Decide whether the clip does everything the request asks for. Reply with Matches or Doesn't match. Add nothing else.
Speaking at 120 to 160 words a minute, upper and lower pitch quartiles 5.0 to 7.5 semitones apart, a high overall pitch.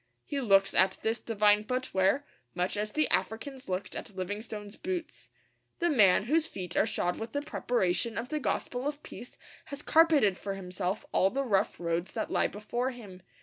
Doesn't match